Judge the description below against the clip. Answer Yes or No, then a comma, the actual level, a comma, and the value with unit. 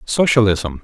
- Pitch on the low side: Yes, low, 110 Hz